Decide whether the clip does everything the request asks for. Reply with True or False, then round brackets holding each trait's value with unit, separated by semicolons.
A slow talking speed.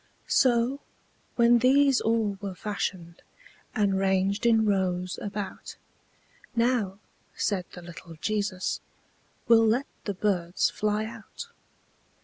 True (110 wpm)